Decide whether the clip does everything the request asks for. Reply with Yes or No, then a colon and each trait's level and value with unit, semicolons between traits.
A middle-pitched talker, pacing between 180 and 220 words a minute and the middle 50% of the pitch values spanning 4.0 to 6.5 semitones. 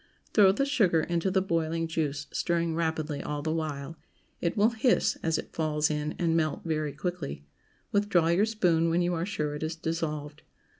No: medium, 165 Hz; average, 185 wpm; narrow, 2.5 semitones